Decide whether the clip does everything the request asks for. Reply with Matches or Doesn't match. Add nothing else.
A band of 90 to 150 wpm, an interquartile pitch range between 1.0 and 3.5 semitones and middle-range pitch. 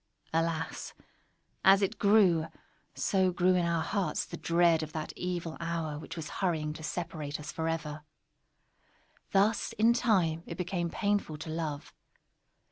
Matches